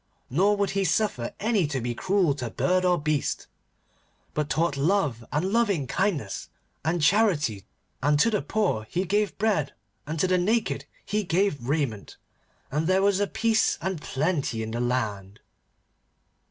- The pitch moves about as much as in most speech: No, wide, 6.6 semitones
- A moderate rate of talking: Yes, average, 155 wpm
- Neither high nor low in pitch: Yes, medium, 165 Hz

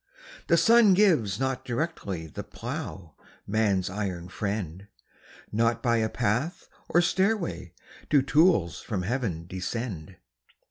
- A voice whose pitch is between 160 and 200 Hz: No, low, 110 Hz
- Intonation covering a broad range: Yes, wide, 8.2 semitones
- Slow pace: Yes, slow, 120 wpm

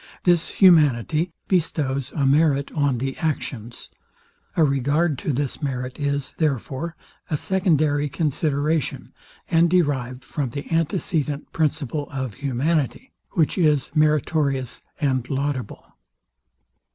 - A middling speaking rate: No, slow, 110 wpm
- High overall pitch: No, medium, 145 Hz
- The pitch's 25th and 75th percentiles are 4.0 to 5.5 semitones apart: No, average, 3.0 semitones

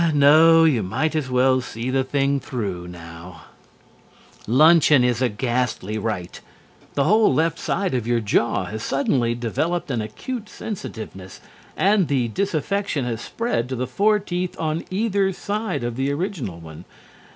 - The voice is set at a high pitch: No, low, 130 Hz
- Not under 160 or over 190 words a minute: No, average, 150 wpm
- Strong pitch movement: Yes, wide, 6.5 semitones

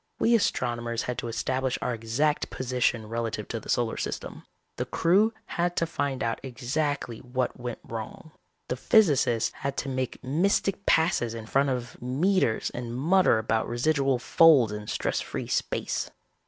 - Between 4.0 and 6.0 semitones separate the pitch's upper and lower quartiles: Yes, average, 4.5 semitones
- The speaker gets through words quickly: No, average, 155 wpm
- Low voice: Yes, low, 125 Hz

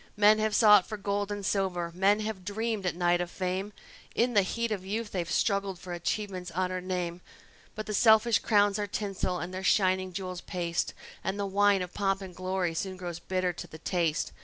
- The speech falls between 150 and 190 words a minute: No, fast, 205 wpm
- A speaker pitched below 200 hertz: Yes, high, 190 Hz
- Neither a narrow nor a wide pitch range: No, narrow, 2.2 semitones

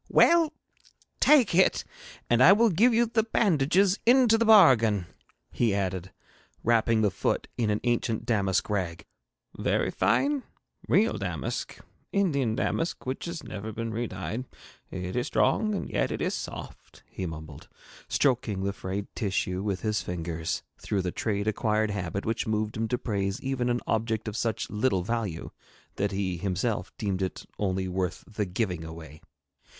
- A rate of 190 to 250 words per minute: No, average, 155 wpm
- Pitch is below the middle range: Yes, low, 110 Hz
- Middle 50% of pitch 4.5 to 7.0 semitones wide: Yes, wide, 5.5 semitones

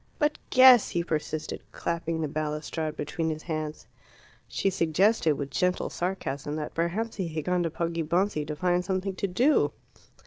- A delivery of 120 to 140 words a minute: No, average, 160 wpm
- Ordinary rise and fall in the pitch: Yes, average, 3.3 semitones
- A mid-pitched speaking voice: Yes, medium, 170 Hz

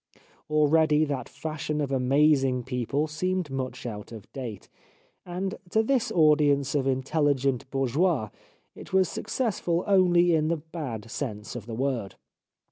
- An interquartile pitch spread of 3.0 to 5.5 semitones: Yes, average, 4.1 semitones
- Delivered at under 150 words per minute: Yes, slow, 135 wpm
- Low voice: No, medium, 145 Hz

